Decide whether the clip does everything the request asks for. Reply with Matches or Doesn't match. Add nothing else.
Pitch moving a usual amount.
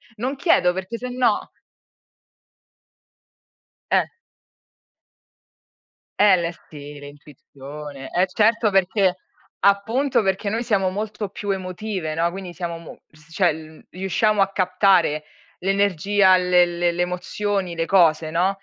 Matches